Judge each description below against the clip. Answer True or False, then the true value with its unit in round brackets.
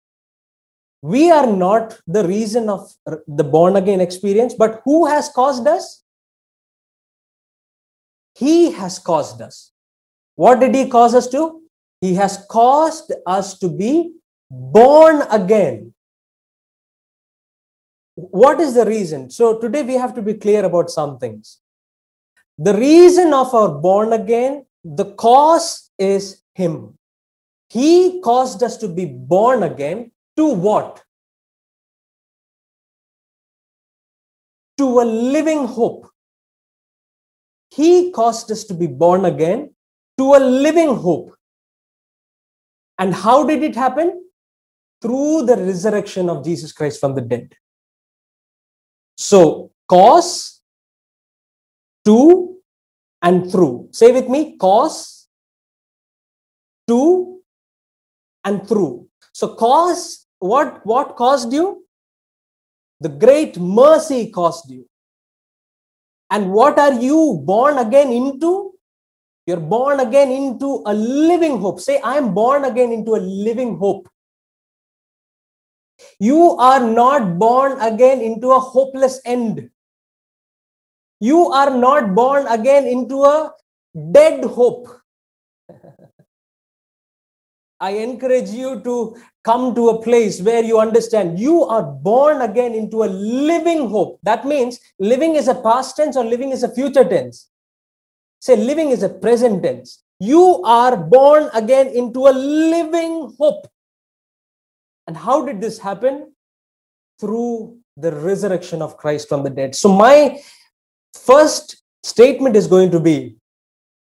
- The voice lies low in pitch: False (240 Hz)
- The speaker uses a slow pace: True (120 wpm)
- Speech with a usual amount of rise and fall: False (6.2 semitones)